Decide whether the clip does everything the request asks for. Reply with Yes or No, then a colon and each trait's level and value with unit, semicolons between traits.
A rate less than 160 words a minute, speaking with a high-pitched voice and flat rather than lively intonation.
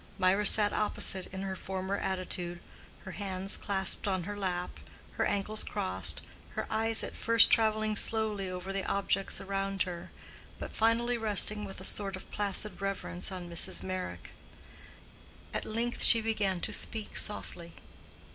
Yes: average, 150 wpm; high, 195 Hz; narrow, 2.3 semitones